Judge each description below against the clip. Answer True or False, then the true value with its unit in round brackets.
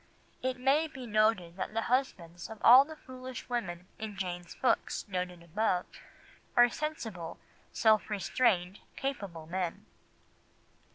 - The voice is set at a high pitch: True (215 Hz)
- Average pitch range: False (6.0 semitones)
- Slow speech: True (125 wpm)